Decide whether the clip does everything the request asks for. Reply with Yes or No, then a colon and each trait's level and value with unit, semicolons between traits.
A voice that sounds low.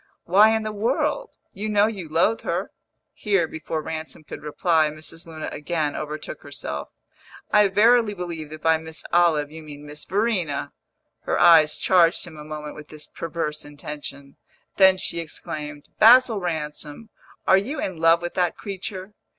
No: medium, 165 Hz